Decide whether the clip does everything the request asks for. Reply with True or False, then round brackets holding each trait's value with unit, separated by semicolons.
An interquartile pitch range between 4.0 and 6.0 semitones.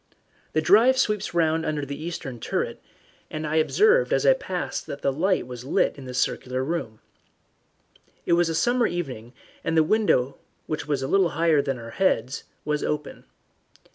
True (4.7 semitones)